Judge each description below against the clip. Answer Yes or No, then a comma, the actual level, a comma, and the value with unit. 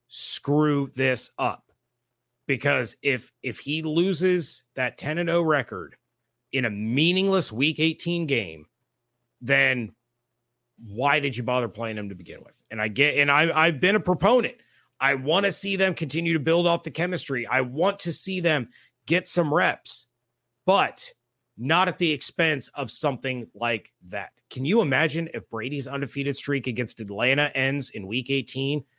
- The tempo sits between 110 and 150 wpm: No, average, 165 wpm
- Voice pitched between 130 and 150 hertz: Yes, medium, 140 Hz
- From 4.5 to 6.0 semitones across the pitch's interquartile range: Yes, average, 5.2 semitones